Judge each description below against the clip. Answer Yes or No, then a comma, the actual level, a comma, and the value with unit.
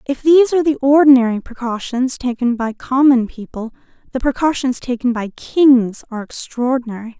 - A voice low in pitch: No, very high, 255 Hz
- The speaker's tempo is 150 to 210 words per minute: No, average, 140 wpm